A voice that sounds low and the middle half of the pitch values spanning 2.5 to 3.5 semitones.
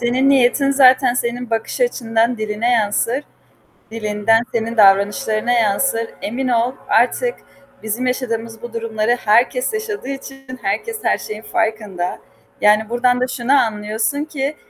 No: high, 235 Hz; average, 3.0 semitones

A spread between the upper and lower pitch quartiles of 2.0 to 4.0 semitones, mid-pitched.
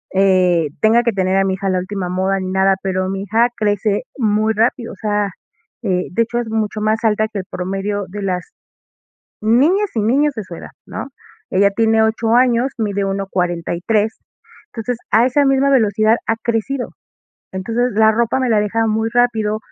No: average, 3.0 semitones; high, 215 Hz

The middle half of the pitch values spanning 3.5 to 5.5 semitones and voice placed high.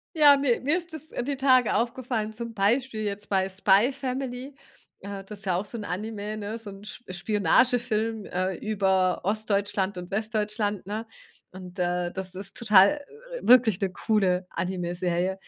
Yes: average, 3.8 semitones; high, 210 Hz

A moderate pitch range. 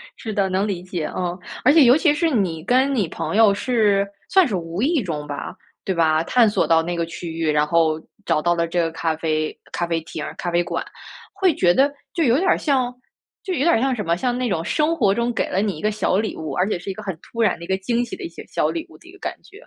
No: wide, 7.1 semitones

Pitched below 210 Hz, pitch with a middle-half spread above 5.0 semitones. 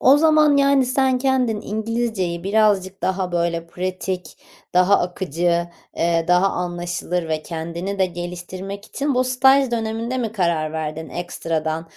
Yes: medium, 185 Hz; wide, 5.4 semitones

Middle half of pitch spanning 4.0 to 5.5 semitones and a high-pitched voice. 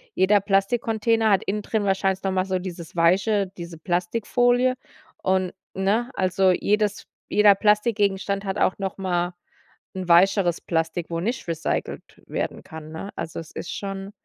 No: average, 2.8 semitones; high, 195 Hz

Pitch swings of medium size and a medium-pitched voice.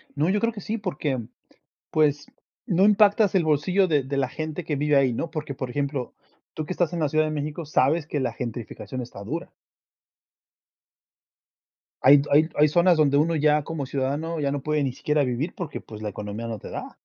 Yes: average, 3.4 semitones; medium, 150 Hz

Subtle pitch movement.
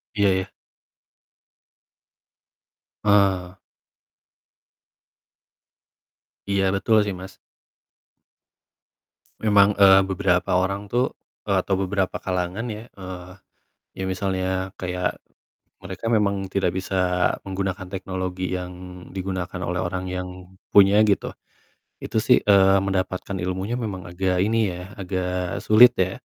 Yes: narrow, 1.4 semitones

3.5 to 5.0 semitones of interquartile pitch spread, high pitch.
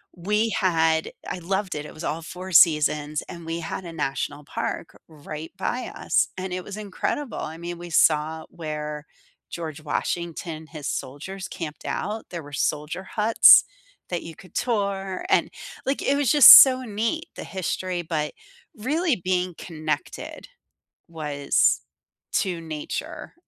No: average, 3.9 semitones; medium, 170 Hz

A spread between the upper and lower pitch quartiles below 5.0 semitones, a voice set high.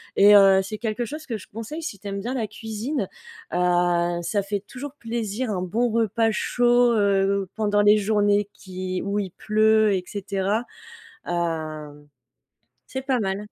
Yes: average, 2.9 semitones; high, 205 Hz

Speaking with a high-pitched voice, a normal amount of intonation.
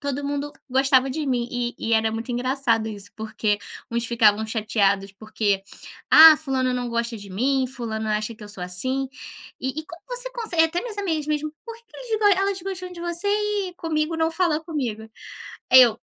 No: very high, 265 Hz; wide, 6.8 semitones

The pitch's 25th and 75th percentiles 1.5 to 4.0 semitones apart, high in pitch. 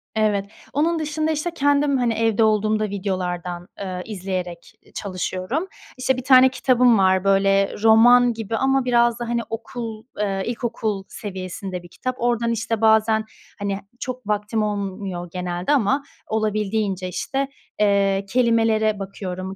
Yes: average, 3.7 semitones; high, 215 Hz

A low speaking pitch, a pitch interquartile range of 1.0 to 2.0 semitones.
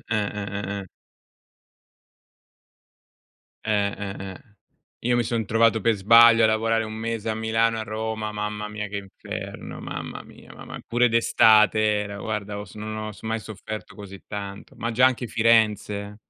Yes: low, 110 Hz; narrow, 1.7 semitones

